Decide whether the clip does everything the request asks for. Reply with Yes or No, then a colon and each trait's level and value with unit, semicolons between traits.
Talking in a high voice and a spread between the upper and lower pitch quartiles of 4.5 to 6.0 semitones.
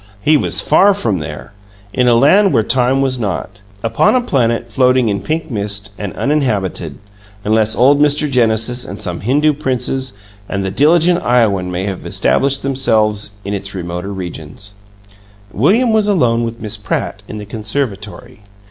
No: low, 115 Hz; average, 5.3 semitones